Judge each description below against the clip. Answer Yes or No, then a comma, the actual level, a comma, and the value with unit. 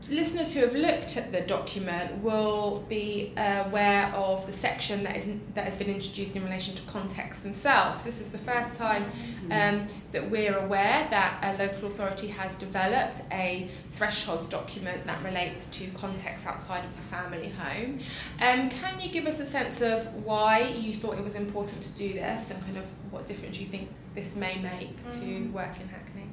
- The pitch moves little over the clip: Yes, narrow, 2.3 semitones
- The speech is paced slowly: No, average, 190 wpm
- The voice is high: Yes, high, 200 Hz